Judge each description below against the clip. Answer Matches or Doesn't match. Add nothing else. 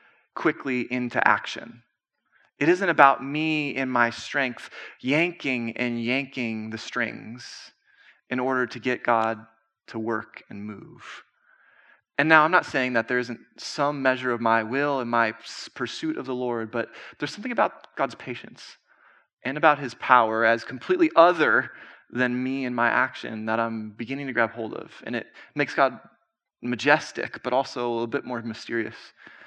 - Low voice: Matches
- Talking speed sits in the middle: Matches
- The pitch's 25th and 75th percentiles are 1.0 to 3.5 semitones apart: Matches